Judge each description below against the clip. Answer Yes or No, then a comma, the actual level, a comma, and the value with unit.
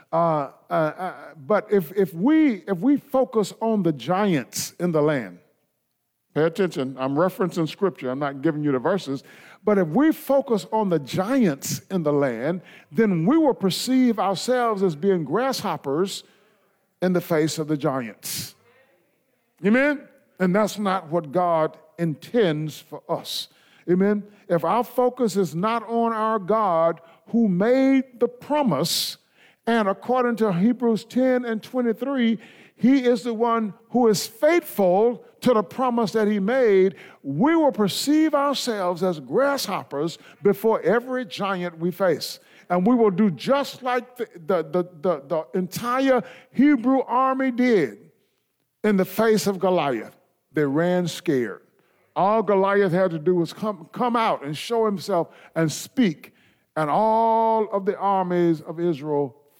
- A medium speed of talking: Yes, average, 150 wpm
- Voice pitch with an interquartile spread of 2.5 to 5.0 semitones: No, wide, 5.5 semitones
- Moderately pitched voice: No, high, 200 Hz